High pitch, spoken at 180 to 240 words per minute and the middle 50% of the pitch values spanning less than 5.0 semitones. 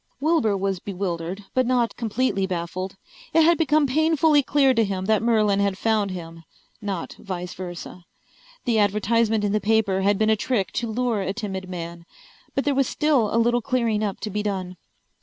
Yes: high, 210 Hz; average, 185 wpm; average, 4.1 semitones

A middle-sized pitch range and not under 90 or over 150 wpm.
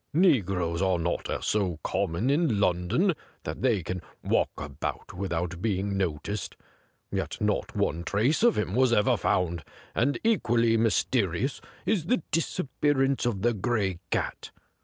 No: wide, 6.6 semitones; average, 140 wpm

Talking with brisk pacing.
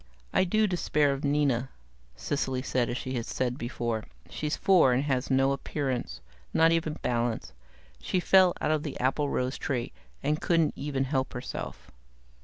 No: average, 160 wpm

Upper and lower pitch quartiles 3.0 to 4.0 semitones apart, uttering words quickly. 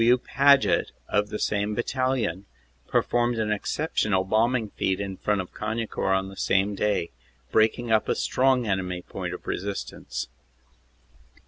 No: average, 3.6 semitones; average, 140 wpm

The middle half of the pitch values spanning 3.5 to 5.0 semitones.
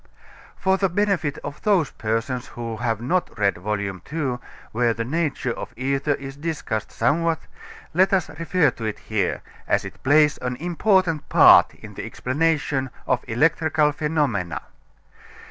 No: wide, 5.5 semitones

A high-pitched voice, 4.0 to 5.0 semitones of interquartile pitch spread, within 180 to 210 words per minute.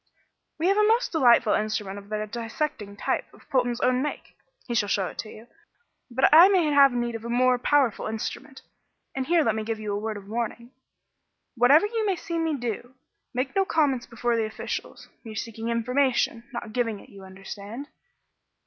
Yes: high, 240 Hz; average, 4.4 semitones; average, 195 wpm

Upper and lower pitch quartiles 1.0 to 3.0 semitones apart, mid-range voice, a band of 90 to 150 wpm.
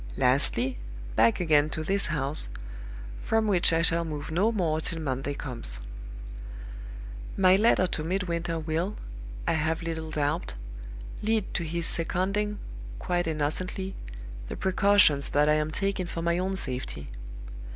No: average, 3.7 semitones; medium, 165 Hz; average, 140 wpm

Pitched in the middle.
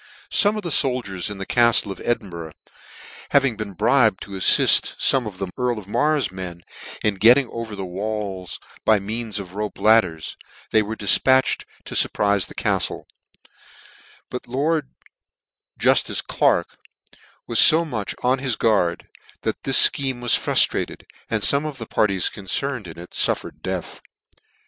No: low, 110 Hz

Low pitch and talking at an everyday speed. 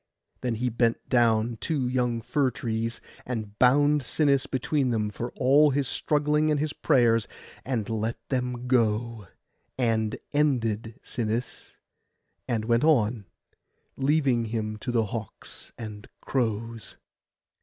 No: low, 120 Hz; slow, 125 wpm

